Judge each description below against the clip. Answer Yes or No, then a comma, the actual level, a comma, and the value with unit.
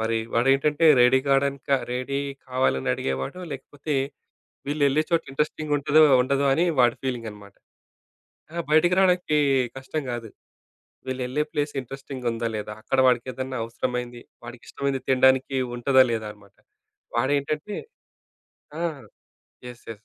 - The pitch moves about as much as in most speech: Yes, average, 3.1 semitones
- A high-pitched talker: No, low, 130 Hz